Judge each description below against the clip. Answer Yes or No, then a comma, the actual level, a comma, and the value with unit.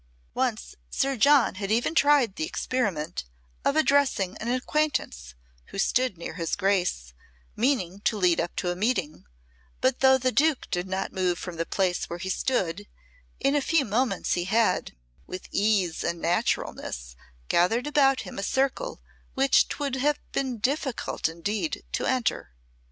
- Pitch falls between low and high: No, high, 210 Hz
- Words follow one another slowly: No, average, 155 wpm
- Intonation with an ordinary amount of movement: No, wide, 6.9 semitones